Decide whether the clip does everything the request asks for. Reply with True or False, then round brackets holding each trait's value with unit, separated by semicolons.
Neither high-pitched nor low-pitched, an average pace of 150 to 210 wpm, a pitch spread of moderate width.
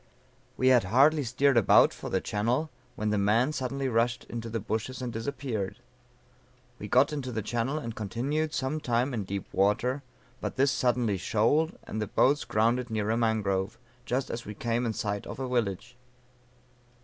False (120 Hz; 175 wpm; 3.3 semitones)